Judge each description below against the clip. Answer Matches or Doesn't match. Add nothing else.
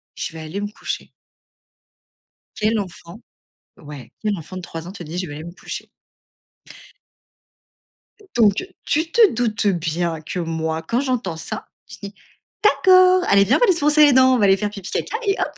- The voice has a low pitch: Doesn't match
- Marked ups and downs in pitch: Matches